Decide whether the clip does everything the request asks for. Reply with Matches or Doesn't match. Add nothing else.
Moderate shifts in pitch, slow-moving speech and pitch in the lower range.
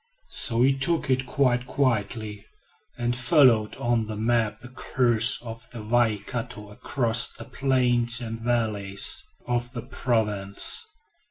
Doesn't match